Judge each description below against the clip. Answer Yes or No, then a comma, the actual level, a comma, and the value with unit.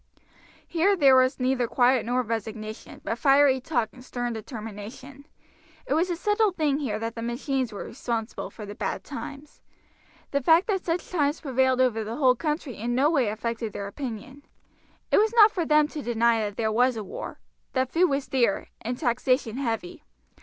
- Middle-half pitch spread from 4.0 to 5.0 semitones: Yes, average, 4.3 semitones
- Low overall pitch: No, very high, 255 Hz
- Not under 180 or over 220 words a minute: Yes, average, 185 wpm